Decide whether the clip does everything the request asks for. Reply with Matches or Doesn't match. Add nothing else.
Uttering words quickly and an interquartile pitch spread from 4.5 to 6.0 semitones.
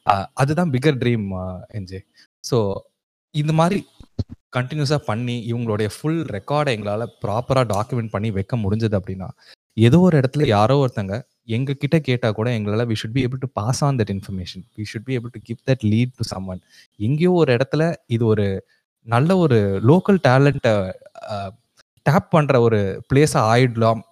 Matches